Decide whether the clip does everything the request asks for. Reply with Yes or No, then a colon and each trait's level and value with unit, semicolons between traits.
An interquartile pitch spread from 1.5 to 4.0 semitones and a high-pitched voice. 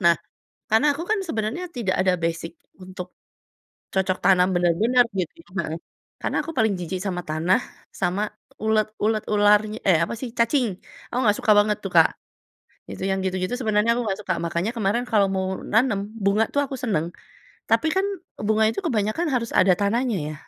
Yes: average, 3.6 semitones; high, 205 Hz